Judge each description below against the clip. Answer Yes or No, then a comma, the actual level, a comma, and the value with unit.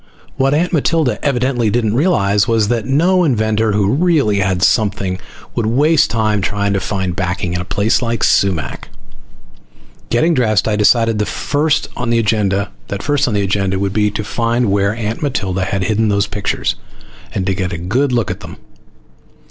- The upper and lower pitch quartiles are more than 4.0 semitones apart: No, average, 3.7 semitones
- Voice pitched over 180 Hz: No, low, 105 Hz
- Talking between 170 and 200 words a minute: No, average, 160 wpm